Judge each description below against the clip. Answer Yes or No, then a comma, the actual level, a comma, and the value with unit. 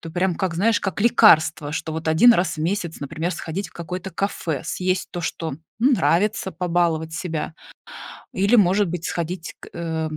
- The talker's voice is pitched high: No, medium, 175 Hz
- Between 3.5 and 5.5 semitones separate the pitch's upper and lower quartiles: No, average, 3.0 semitones